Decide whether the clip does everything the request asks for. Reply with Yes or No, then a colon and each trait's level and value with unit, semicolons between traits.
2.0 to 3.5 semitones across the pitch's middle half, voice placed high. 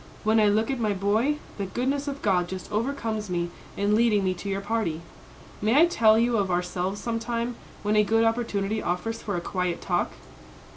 Yes: average, 3.1 semitones; high, 215 Hz